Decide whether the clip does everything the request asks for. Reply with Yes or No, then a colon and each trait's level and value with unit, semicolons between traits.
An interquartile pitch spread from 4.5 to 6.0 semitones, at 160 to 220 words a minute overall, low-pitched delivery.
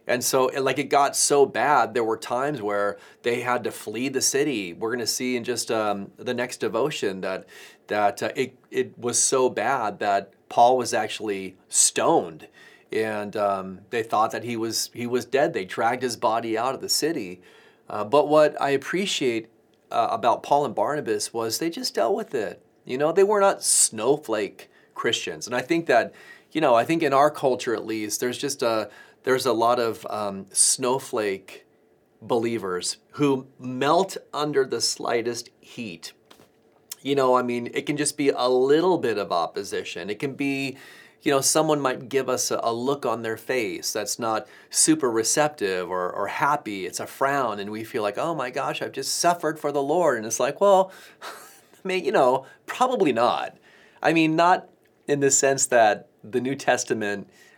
Yes: average, 4.8 semitones; average, 190 wpm; low, 130 Hz